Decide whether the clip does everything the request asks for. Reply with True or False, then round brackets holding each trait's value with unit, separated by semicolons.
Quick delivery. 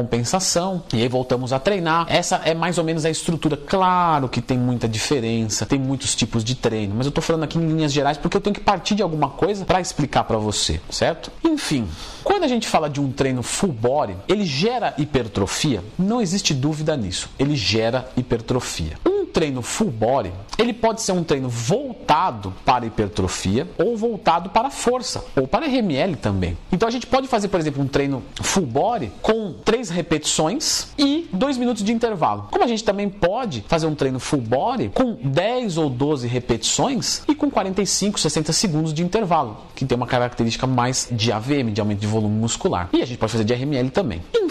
True (195 wpm)